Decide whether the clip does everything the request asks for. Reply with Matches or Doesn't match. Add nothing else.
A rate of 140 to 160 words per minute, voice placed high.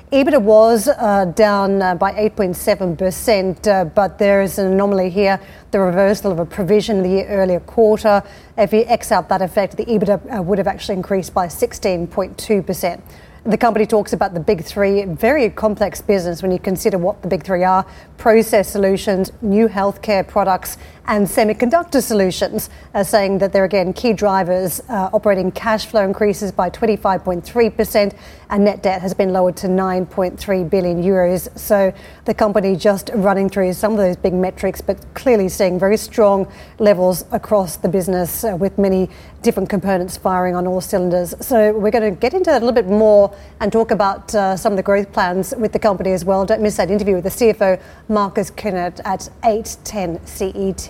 Doesn't match